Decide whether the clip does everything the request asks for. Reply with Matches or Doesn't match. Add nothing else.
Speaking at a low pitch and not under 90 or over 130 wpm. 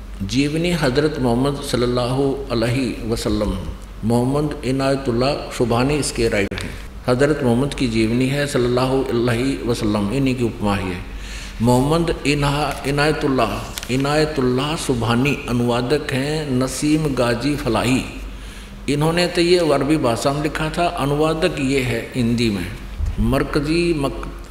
Matches